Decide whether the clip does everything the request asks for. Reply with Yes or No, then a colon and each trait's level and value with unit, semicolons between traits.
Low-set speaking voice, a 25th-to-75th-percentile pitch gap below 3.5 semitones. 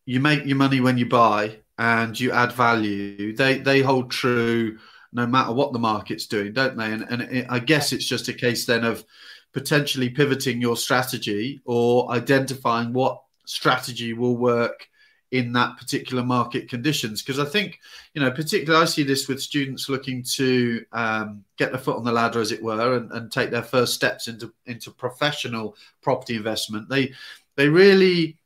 Yes: low, 125 Hz; narrow, 2.6 semitones